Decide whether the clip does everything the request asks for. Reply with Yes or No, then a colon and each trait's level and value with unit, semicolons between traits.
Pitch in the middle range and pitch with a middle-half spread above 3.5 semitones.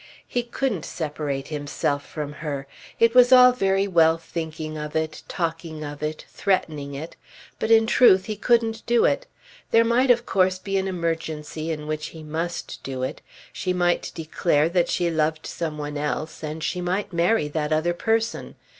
Yes: medium, 165 Hz; average, 4.3 semitones